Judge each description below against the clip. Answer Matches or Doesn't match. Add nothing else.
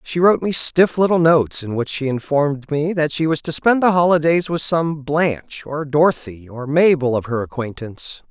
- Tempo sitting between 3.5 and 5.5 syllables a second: Matches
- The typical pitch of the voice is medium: Matches